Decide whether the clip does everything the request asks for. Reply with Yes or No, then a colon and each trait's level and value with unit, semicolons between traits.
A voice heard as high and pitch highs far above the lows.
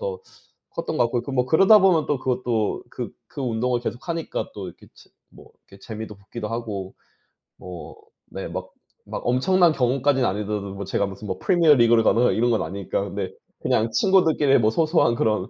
No: low, 120 Hz; wide, 6.0 semitones